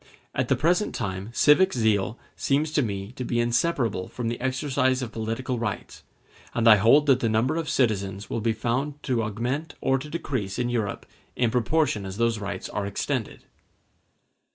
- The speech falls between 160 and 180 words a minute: Yes, average, 175 wpm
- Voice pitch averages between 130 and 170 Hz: No, low, 120 Hz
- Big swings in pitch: No, average, 3.7 semitones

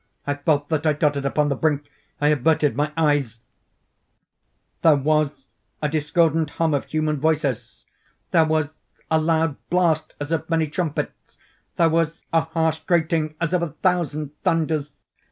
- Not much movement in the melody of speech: Yes, narrow, 1.8 semitones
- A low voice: No, medium, 155 Hz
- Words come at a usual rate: Yes, average, 150 wpm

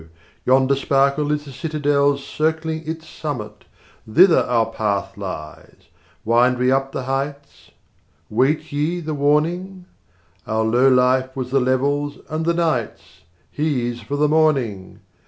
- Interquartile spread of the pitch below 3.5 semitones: No, average, 3.8 semitones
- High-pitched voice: No, medium, 140 Hz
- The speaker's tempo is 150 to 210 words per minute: No, slow, 135 wpm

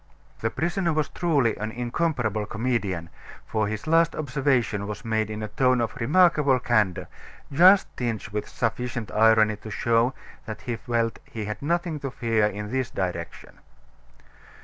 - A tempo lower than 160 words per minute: Yes, average, 150 wpm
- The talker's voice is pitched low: Yes, low, 115 Hz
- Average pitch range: Yes, average, 4.3 semitones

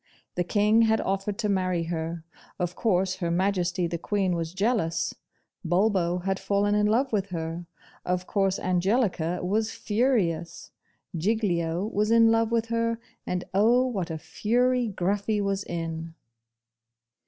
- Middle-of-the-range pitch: No, high, 195 Hz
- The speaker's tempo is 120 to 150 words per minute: Yes, average, 140 wpm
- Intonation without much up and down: No, average, 3.9 semitones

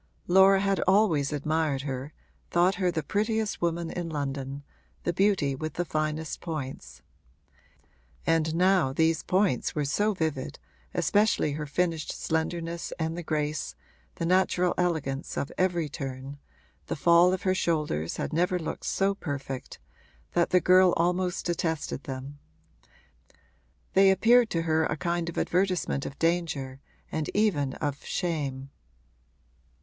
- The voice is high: No, medium, 165 Hz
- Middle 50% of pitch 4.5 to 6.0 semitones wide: No, average, 3.7 semitones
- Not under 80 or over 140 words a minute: Yes, slow, 135 wpm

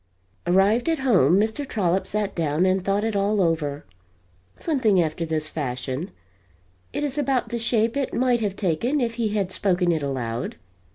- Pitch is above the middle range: Yes, high, 195 Hz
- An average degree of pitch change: No, wide, 6.0 semitones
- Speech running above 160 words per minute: Yes, average, 170 wpm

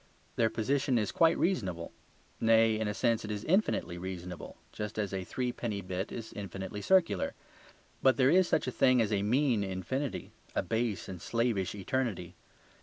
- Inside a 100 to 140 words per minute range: No, average, 170 wpm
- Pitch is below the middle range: Yes, low, 110 Hz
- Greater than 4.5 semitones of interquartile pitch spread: Yes, average, 4.9 semitones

